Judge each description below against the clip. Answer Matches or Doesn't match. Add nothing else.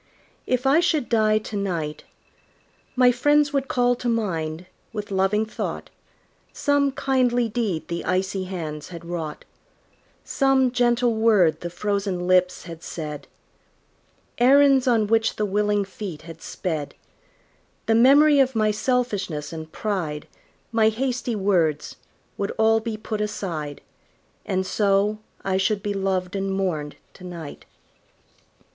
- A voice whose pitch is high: Matches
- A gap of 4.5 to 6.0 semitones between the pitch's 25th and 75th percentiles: Matches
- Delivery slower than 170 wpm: Matches